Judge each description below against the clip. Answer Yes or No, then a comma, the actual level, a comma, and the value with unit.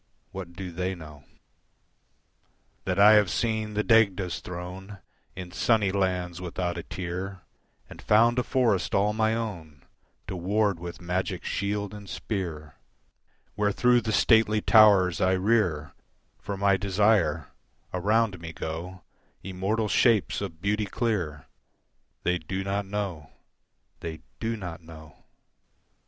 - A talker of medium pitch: No, very low, 95 Hz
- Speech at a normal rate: No, slow, 130 wpm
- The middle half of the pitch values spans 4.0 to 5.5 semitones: No, average, 3.2 semitones